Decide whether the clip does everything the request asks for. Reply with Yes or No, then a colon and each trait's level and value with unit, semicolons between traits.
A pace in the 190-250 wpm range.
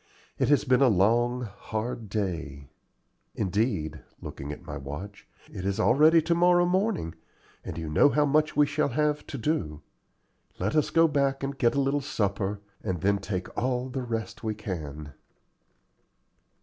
No: average, 160 wpm